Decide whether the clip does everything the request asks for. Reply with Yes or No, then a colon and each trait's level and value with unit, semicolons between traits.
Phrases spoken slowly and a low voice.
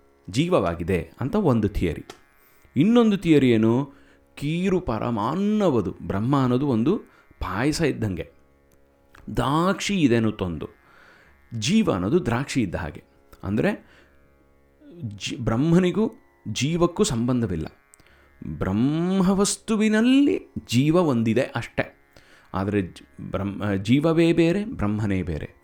No: average, 85 wpm; low, 115 Hz